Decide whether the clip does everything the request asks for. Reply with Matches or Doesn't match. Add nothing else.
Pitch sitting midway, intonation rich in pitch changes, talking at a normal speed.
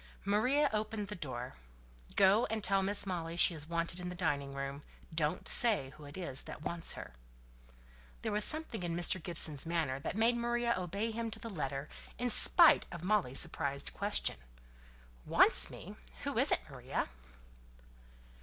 Matches